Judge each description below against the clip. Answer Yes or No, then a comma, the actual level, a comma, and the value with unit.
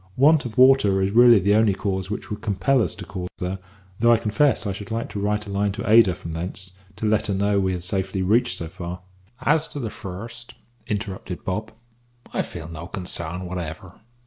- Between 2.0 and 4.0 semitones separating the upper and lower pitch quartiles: Yes, average, 3.4 semitones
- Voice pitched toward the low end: Yes, low, 100 Hz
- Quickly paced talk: Yes, fast, 215 wpm